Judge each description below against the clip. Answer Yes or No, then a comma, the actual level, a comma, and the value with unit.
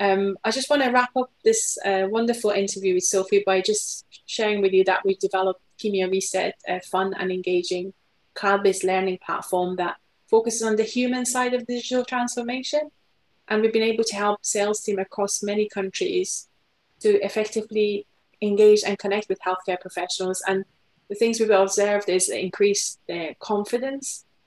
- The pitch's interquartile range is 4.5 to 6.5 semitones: No, average, 2.9 semitones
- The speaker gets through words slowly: No, average, 165 wpm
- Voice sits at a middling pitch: No, high, 205 Hz